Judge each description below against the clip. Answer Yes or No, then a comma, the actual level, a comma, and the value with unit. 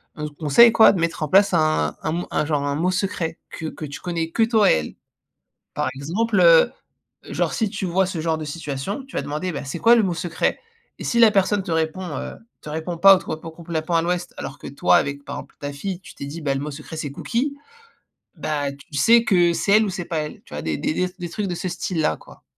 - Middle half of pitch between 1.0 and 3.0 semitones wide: No, average, 4.2 semitones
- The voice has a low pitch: No, medium, 170 Hz